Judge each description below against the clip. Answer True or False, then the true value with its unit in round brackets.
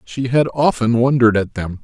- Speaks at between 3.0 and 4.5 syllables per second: False (5.4 syllables/s)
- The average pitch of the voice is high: False (120 Hz)